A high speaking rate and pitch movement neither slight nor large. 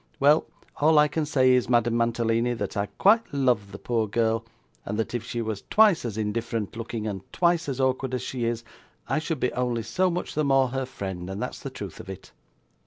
Yes: fast, 220 wpm; average, 3.7 semitones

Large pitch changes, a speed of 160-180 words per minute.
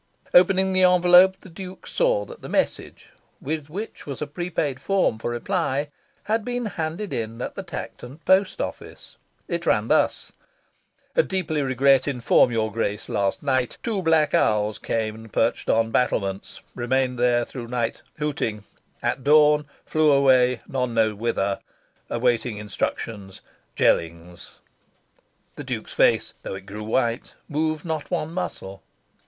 No: wide, 6.7 semitones; average, 145 wpm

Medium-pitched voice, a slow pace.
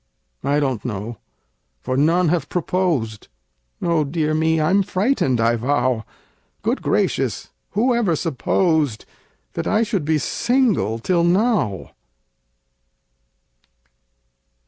Yes: medium, 160 Hz; slow, 105 wpm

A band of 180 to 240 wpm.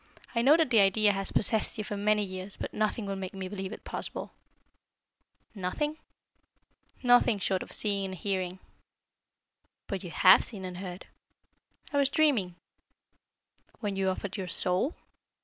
No: average, 155 wpm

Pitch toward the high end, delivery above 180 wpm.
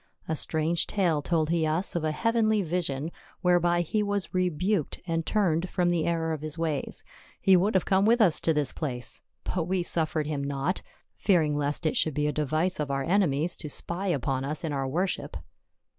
No: medium, 165 Hz; fast, 205 wpm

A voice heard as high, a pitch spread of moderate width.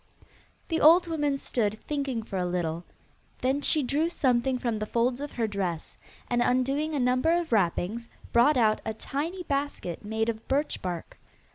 Yes: very high, 250 Hz; average, 5.0 semitones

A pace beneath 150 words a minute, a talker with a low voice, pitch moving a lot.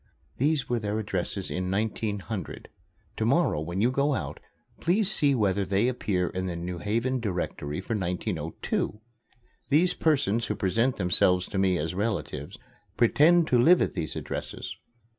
No: average, 155 wpm; low, 105 Hz; wide, 5.8 semitones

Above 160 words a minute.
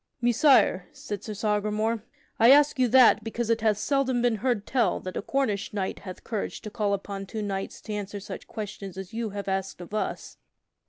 Yes: average, 200 wpm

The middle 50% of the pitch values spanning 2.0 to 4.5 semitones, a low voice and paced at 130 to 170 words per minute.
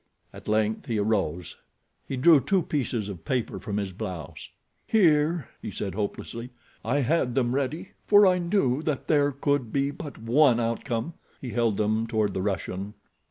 No: average, 5.3 semitones; low, 120 Hz; average, 165 wpm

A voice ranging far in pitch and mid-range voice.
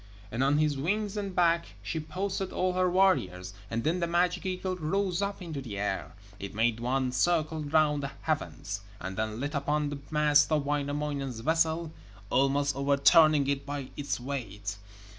No: average, 4.1 semitones; medium, 145 Hz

